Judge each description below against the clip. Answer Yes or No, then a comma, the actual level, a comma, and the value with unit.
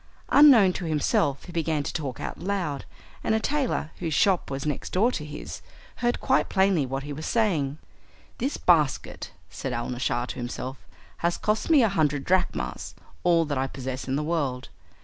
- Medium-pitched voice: Yes, medium, 155 Hz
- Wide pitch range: Yes, wide, 6.1 semitones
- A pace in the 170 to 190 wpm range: Yes, average, 180 wpm